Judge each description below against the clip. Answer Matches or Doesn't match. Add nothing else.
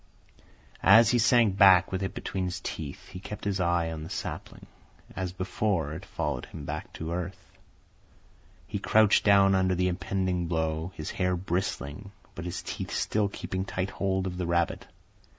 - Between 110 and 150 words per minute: Doesn't match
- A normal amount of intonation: Doesn't match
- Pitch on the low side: Matches